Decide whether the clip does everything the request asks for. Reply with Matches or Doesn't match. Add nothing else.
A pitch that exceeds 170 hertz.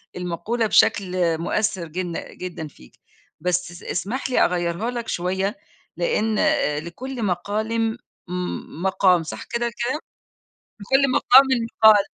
Matches